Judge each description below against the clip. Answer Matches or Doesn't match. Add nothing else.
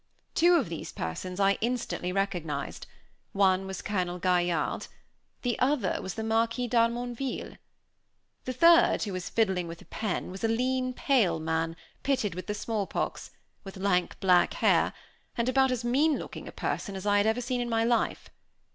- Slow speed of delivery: Doesn't match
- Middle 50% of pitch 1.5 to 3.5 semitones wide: Doesn't match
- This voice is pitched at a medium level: Doesn't match